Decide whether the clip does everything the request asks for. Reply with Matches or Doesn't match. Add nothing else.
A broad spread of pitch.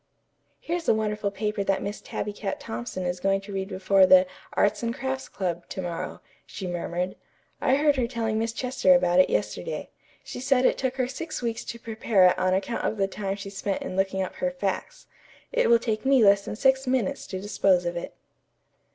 Doesn't match